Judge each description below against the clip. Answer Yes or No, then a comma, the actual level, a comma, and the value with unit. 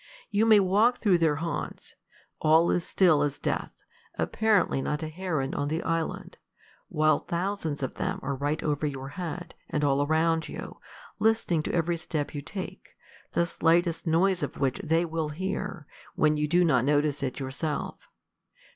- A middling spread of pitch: Yes, average, 3.2 semitones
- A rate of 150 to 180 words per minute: Yes, average, 165 wpm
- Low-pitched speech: No, medium, 160 Hz